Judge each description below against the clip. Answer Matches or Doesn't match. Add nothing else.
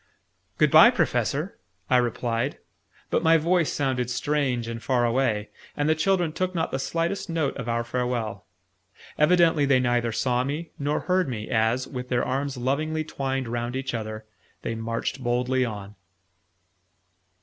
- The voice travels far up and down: Doesn't match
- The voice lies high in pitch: Doesn't match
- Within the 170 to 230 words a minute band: Doesn't match